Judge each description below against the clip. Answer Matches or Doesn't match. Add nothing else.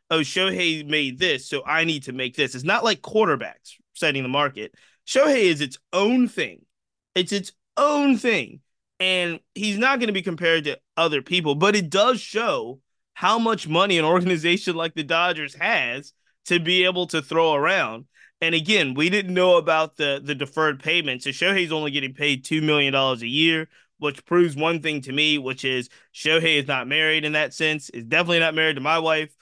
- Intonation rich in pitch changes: Doesn't match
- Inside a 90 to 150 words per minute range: Doesn't match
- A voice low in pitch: Doesn't match